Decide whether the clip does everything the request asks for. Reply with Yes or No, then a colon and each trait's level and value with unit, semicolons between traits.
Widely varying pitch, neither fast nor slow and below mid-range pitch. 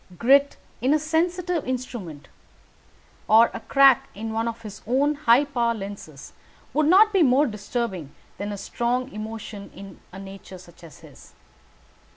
No: wide, 5.9 semitones; average, 155 wpm; high, 235 Hz